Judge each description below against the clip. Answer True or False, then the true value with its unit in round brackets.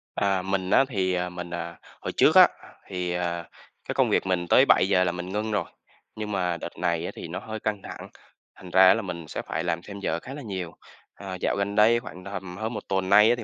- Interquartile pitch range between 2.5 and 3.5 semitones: True (2.8 semitones)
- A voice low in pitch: True (95 Hz)